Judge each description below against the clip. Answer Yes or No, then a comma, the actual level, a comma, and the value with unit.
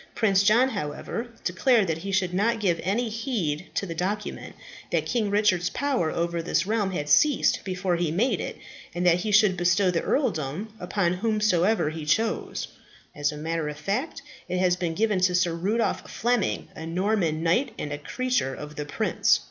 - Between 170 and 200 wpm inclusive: Yes, average, 185 wpm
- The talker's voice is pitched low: No, medium, 185 Hz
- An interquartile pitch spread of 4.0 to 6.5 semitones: Yes, average, 4.6 semitones